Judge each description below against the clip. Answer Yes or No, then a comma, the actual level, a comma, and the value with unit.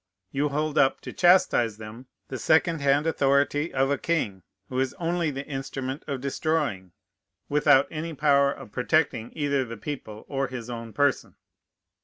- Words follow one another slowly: No, average, 160 wpm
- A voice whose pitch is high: No, medium, 140 Hz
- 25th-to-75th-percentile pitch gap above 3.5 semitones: No, average, 2.9 semitones